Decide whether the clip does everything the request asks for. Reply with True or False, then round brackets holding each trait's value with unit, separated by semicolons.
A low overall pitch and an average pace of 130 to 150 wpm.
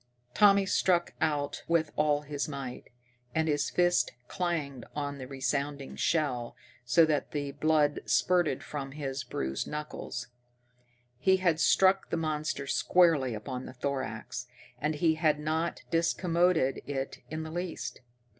False (150 Hz; 135 wpm)